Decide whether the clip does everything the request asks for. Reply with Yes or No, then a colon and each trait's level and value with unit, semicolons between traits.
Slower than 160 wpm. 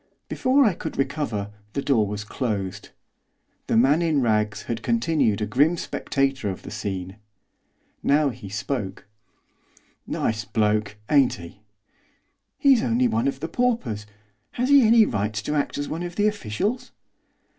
Yes: average, 150 wpm